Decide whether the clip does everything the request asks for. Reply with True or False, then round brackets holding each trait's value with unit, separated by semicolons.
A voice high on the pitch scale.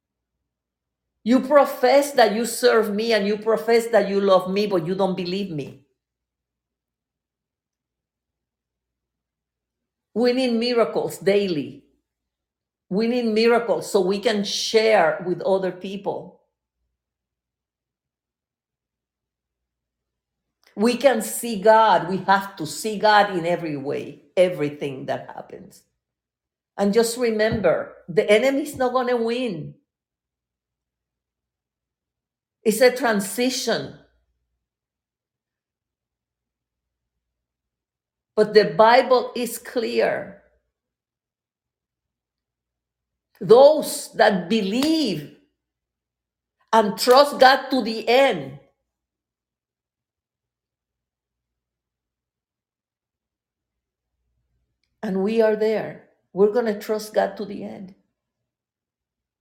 True (205 Hz)